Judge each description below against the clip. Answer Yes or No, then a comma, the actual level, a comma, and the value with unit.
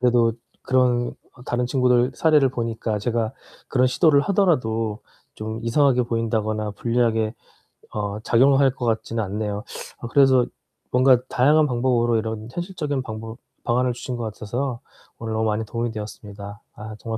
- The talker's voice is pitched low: Yes, low, 120 Hz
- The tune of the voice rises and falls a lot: No, narrow, 2.6 semitones